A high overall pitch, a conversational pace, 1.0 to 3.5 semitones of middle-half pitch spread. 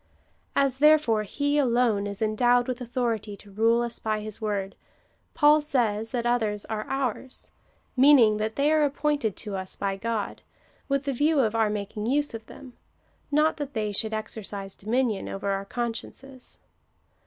No: high, 230 Hz; average, 175 wpm; average, 4.2 semitones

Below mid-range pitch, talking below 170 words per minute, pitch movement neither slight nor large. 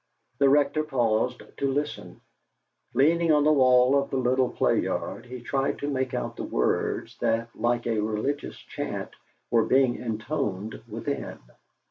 Yes: low, 130 Hz; average, 150 wpm; average, 3.3 semitones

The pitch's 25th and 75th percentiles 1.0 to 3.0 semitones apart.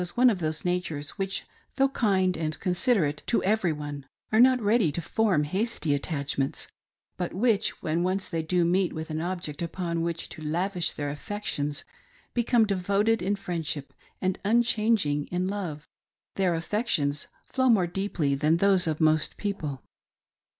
No: average, 4.7 semitones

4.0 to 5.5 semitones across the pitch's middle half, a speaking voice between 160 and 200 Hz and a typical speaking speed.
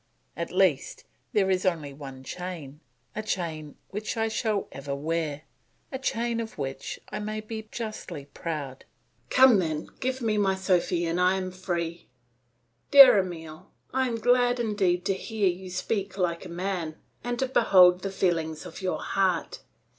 Yes: average, 4.5 semitones; medium, 185 Hz; average, 160 wpm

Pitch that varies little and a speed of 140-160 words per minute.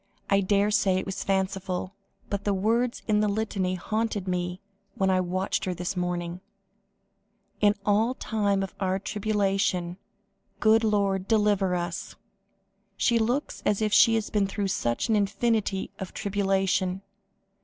Yes: narrow, 2.2 semitones; average, 145 wpm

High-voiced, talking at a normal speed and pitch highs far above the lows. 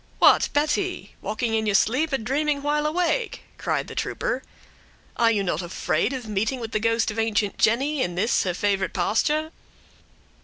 Yes: high, 230 Hz; average, 175 wpm; wide, 6.1 semitones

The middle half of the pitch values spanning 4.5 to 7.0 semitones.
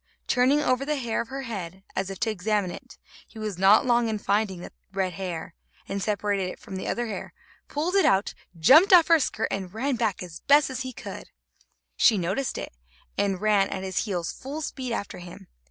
Yes: average, 5.2 semitones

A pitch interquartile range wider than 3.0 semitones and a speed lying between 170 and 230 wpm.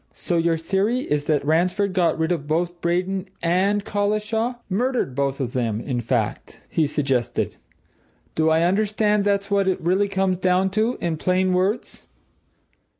No: average, 4.0 semitones; average, 150 wpm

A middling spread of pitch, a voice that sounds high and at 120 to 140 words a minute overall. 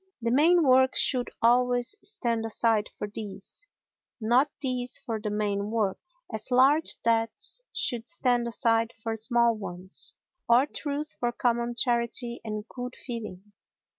No: narrow, 2.3 semitones; high, 235 Hz; slow, 135 wpm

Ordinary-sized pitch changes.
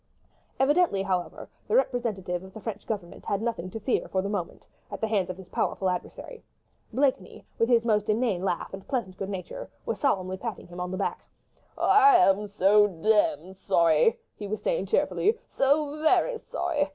No: wide, 6.0 semitones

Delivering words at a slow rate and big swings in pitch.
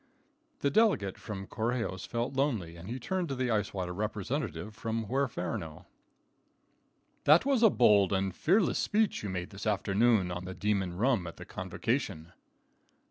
No: average, 155 wpm; wide, 5.7 semitones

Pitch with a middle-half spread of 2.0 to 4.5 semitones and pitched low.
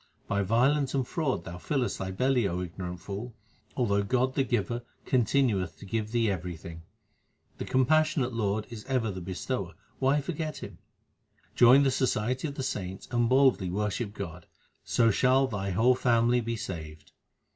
No: average, 4.9 semitones; low, 115 Hz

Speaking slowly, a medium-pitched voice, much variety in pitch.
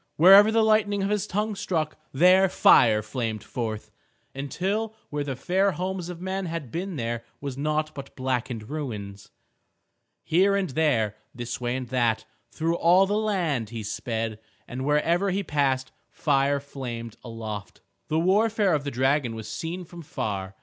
No: average, 160 wpm; medium, 145 Hz; wide, 7.6 semitones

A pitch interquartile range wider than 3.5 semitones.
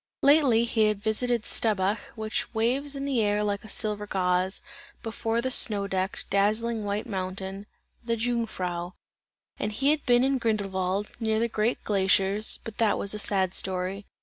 No: average, 2.9 semitones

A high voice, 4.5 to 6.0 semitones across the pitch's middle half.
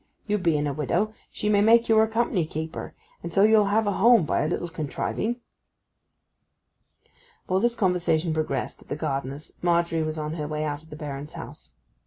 No: medium, 170 Hz; wide, 5.4 semitones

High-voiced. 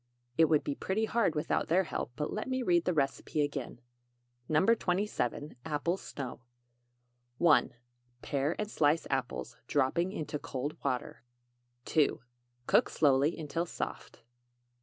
No: medium, 155 Hz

